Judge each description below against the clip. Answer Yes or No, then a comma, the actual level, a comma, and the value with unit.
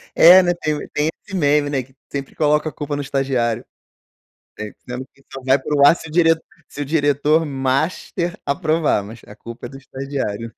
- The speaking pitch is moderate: Yes, medium, 145 Hz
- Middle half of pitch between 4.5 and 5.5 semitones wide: No, average, 2.8 semitones